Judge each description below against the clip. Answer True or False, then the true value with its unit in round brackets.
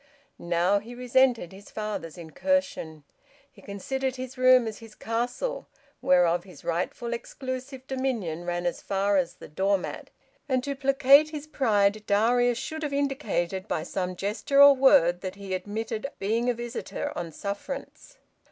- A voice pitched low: False (225 Hz)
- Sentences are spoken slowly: False (150 wpm)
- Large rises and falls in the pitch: True (5.8 semitones)